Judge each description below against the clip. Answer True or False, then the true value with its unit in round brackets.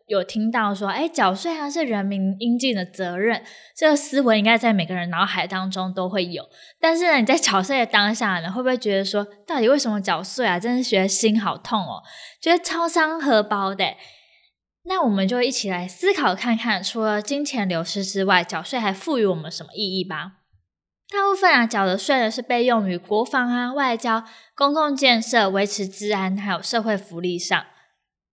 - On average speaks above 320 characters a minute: False (290 characters per minute)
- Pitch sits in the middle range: False (215 Hz)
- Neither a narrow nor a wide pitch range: True (4.9 semitones)